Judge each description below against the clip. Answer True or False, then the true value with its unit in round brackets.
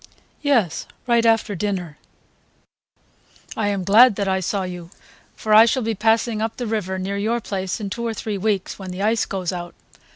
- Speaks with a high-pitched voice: True (205 Hz)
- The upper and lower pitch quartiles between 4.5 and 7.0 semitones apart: False (3.0 semitones)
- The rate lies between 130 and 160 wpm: False (190 wpm)